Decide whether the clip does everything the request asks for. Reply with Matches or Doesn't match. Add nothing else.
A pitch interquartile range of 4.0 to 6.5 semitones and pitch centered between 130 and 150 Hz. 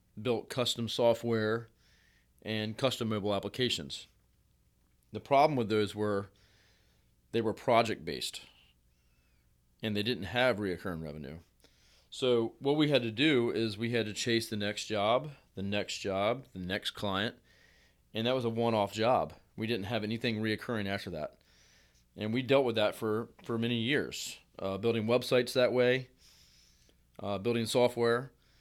Doesn't match